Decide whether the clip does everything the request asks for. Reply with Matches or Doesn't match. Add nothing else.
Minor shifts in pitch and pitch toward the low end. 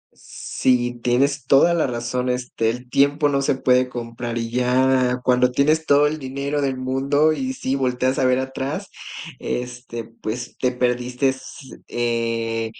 Matches